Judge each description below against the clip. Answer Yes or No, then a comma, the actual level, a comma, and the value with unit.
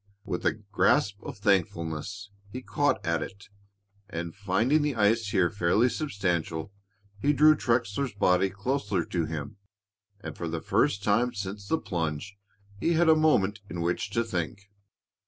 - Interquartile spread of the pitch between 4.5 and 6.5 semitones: Yes, average, 4.8 semitones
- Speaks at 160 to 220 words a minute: No, average, 150 wpm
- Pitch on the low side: Yes, low, 100 Hz